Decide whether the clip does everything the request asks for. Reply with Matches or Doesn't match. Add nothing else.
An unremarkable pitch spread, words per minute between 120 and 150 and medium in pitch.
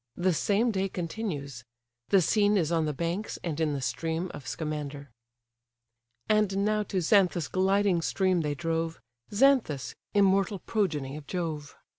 Matches